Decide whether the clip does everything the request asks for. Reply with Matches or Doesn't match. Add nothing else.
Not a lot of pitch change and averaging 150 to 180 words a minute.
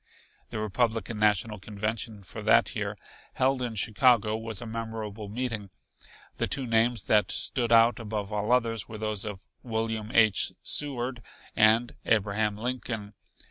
Doesn't match